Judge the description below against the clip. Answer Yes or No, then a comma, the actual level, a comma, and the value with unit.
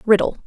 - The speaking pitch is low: No, high, 205 Hz